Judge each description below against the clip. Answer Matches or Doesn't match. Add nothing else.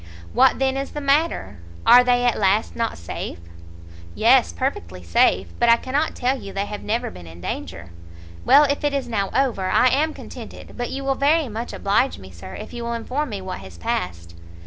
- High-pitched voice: Matches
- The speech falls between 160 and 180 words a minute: Doesn't match